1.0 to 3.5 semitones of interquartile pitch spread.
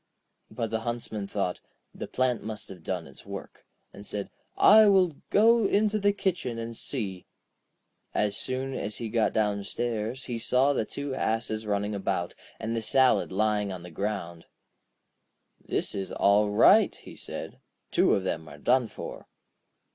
No: average, 4.3 semitones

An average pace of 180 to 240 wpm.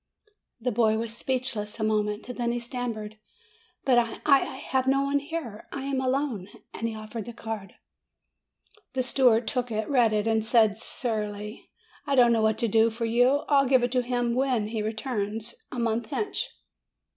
Yes: average, 185 wpm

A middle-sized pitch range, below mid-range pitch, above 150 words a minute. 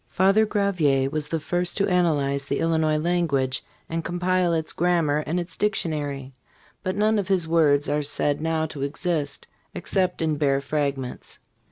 No: average, 3.6 semitones; medium, 160 Hz; average, 160 wpm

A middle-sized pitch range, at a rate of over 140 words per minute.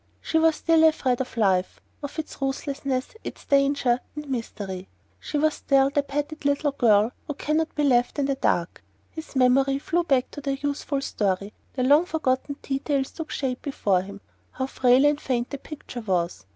Yes: average, 3.0 semitones; average, 180 wpm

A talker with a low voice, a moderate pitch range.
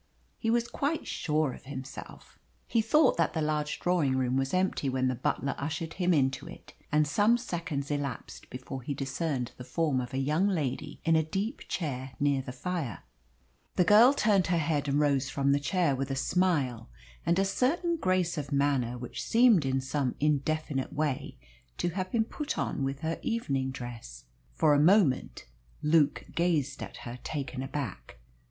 No: medium, 150 Hz; average, 4.9 semitones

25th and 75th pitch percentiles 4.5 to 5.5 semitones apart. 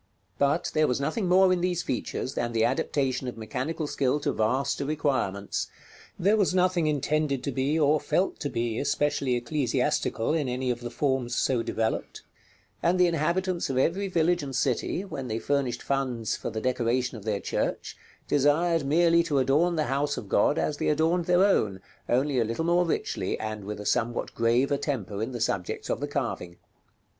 Yes: average, 5.1 semitones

